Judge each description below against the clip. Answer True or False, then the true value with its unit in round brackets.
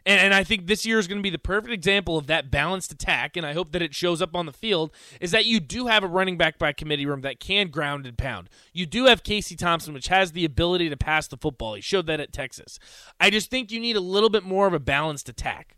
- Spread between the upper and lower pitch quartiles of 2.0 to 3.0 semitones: False (4.7 semitones)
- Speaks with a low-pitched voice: False (175 Hz)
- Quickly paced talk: True (280 wpm)